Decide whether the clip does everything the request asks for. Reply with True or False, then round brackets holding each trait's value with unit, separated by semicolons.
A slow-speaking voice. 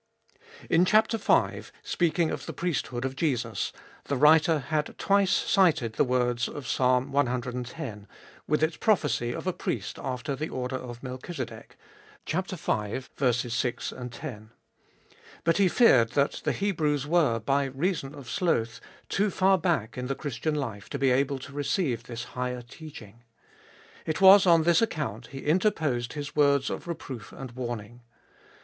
False (150 wpm)